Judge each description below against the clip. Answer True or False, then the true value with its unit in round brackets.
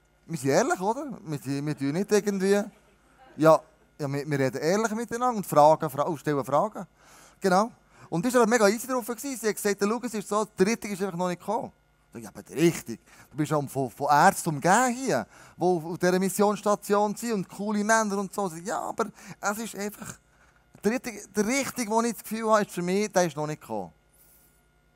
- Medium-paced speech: False (210 wpm)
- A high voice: True (200 Hz)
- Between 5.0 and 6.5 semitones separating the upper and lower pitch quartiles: True (5.4 semitones)